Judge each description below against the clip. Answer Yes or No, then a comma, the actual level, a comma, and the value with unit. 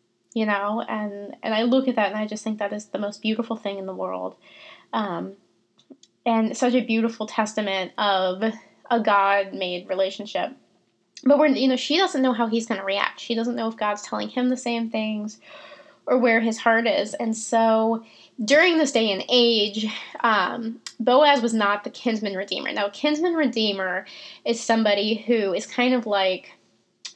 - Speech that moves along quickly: No, average, 185 wpm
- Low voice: No, high, 225 Hz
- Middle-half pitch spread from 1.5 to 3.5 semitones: Yes, average, 3.0 semitones